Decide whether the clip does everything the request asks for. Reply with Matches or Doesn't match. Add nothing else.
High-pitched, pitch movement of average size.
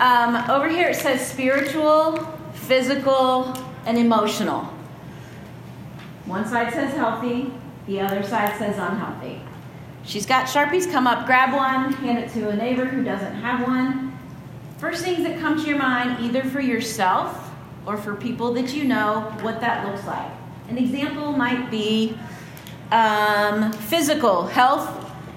Matches